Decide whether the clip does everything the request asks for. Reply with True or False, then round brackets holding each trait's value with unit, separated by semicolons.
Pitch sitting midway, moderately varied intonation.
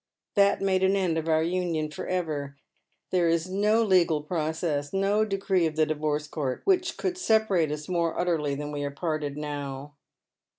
True (165 Hz; 4.0 semitones)